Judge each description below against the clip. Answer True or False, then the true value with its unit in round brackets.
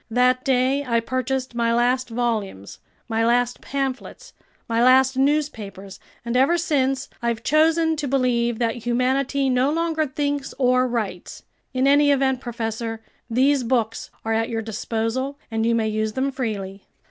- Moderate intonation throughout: True (3.0 semitones)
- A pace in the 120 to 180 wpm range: True (150 wpm)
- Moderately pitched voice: False (250 Hz)